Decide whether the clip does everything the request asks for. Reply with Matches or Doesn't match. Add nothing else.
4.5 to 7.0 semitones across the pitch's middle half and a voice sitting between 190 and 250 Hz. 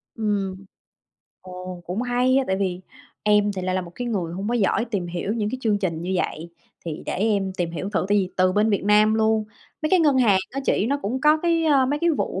Matches